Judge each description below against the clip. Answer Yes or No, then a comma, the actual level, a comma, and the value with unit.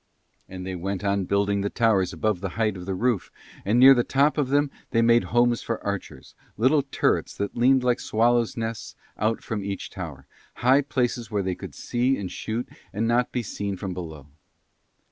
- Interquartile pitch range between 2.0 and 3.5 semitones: No, average, 3.9 semitones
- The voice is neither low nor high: No, low, 110 Hz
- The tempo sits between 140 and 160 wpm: No, average, 195 wpm